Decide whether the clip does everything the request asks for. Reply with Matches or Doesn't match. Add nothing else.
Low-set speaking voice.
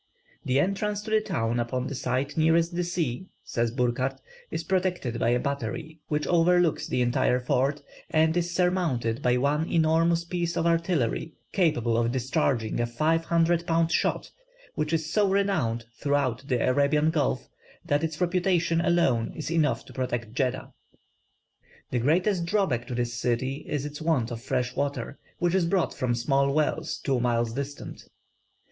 Doesn't match